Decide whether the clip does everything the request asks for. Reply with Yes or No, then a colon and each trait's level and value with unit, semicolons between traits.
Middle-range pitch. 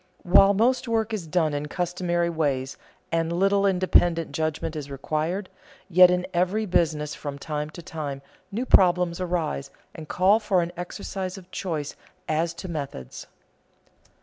Yes: medium, 170 Hz